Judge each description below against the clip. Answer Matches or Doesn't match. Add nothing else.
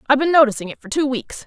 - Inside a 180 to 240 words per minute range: Doesn't match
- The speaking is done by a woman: Matches